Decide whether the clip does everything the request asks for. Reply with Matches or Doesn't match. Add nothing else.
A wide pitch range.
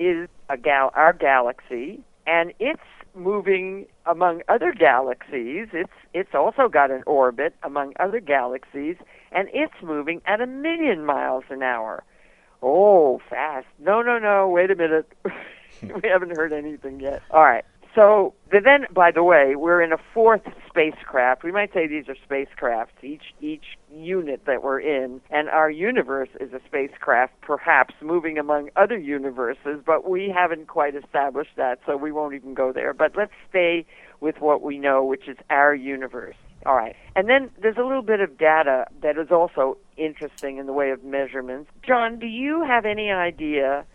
Matches